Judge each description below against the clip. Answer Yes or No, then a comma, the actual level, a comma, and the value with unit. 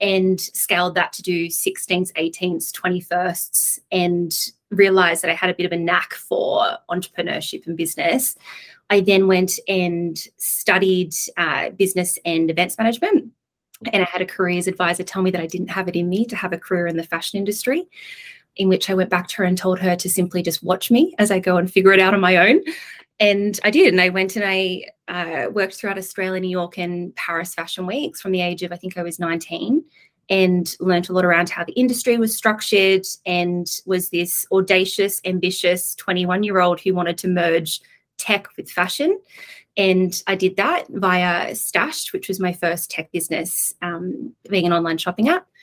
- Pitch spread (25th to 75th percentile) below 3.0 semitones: Yes, narrow, 2.4 semitones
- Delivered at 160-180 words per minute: No, average, 195 wpm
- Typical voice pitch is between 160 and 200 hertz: Yes, medium, 185 Hz